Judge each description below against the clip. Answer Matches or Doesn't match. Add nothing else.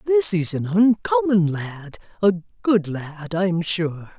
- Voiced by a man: Doesn't match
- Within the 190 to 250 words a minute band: Doesn't match